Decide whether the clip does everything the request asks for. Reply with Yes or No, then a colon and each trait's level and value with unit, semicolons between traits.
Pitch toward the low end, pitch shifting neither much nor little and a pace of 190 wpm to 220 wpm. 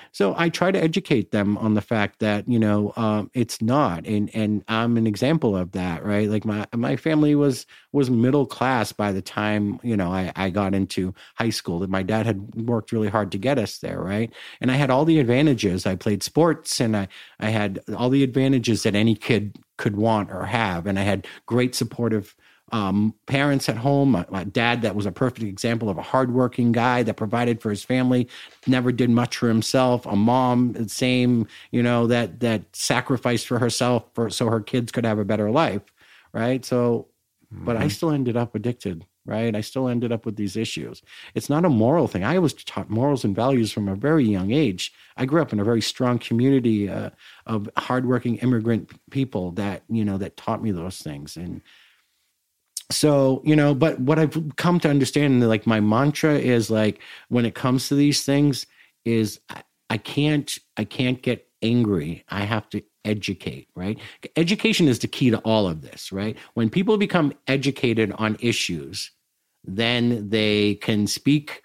Yes: low, 115 Hz; average, 3.5 semitones; average, 195 wpm